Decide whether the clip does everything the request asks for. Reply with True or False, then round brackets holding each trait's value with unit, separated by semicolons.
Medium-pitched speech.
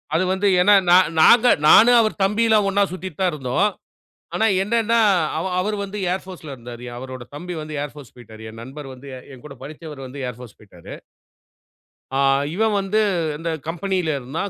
True (165 Hz)